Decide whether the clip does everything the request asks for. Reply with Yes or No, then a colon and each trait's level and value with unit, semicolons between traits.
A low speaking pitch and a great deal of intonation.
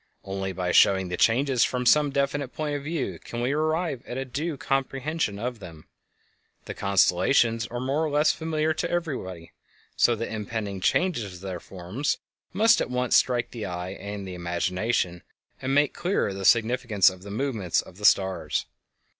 Yes: low, 120 Hz; wide, 6.7 semitones